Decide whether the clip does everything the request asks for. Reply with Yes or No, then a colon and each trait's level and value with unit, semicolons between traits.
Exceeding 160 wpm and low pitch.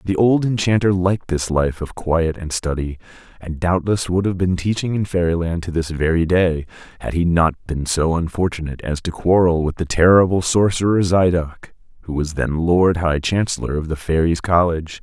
Yes: average, 185 wpm; very low, 85 Hz